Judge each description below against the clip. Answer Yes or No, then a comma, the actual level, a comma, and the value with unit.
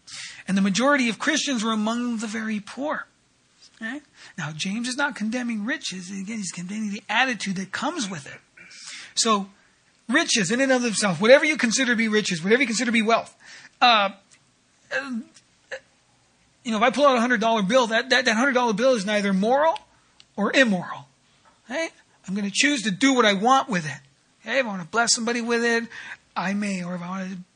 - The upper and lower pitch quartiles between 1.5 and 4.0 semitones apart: No, average, 4.4 semitones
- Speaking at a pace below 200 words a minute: No, fast, 205 wpm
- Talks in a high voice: Yes, high, 230 Hz